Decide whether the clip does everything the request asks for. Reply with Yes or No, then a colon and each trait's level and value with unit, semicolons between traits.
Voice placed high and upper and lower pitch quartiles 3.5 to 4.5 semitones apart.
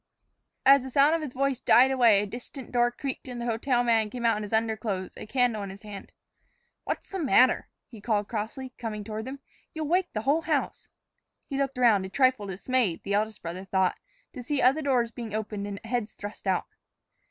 Yes: high, 235 Hz; average, 3.9 semitones